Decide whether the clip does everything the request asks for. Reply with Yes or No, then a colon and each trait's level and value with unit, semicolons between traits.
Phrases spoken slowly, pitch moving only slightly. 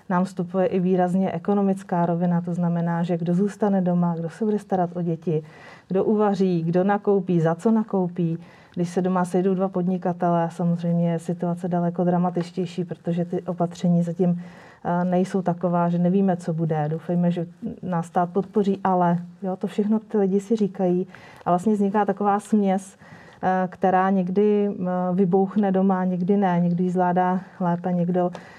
No: average, 155 wpm; narrow, 1.8 semitones